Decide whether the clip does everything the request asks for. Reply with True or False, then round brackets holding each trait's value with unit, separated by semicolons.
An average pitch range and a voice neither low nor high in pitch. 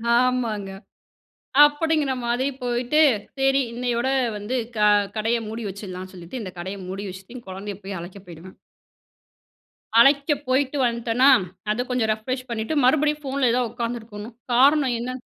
False (4.0 semitones; 240 Hz)